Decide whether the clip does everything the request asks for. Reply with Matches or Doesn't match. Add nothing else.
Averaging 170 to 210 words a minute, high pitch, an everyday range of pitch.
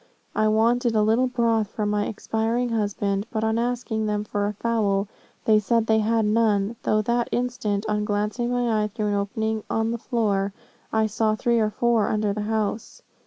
Doesn't match